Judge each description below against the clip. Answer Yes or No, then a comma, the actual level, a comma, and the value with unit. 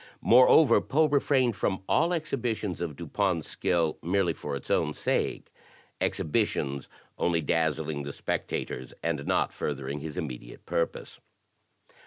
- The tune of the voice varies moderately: No, wide, 6.8 semitones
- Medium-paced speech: Yes, average, 145 wpm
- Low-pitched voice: Yes, very low, 85 Hz